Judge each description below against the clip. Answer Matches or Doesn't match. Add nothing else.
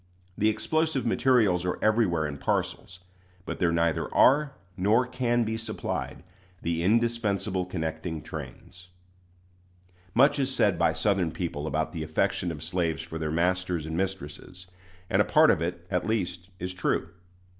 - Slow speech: Doesn't match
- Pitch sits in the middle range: Doesn't match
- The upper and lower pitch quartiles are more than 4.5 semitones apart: Matches